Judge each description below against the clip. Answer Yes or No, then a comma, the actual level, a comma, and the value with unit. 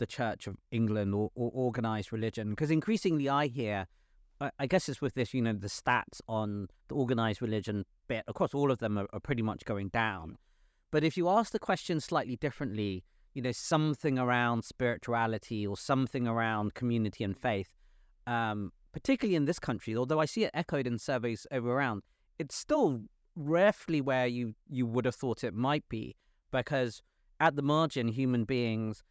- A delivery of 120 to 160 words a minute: No, average, 180 wpm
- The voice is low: Yes, low, 125 Hz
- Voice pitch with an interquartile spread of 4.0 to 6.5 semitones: Yes, average, 4.5 semitones